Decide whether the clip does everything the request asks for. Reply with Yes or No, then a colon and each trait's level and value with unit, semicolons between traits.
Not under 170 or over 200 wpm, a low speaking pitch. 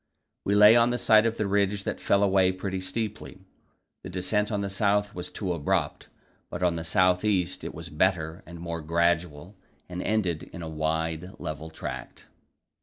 Yes: average, 180 wpm; very low, 95 Hz